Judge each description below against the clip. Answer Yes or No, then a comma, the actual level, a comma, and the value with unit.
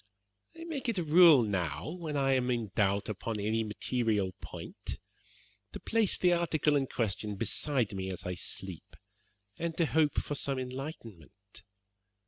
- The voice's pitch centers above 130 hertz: No, low, 125 Hz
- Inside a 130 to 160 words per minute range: Yes, average, 155 wpm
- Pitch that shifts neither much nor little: No, wide, 7.5 semitones